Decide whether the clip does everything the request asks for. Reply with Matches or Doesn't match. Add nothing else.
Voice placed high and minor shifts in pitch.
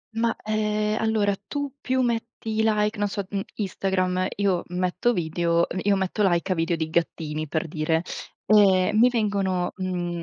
Doesn't match